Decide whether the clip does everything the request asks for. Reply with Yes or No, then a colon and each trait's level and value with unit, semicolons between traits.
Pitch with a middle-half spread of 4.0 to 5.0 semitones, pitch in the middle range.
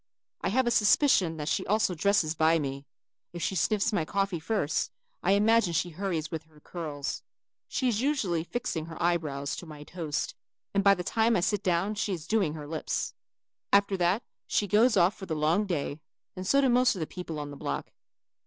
Yes: average, 4.7 semitones; medium, 180 Hz